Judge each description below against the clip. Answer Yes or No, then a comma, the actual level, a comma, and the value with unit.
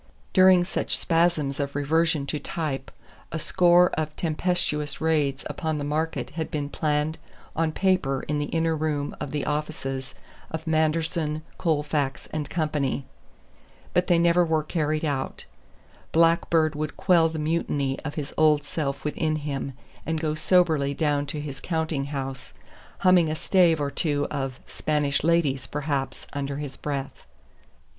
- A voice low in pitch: No, medium, 155 Hz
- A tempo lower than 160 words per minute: Yes, average, 150 wpm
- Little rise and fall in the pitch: Yes, narrow, 2.2 semitones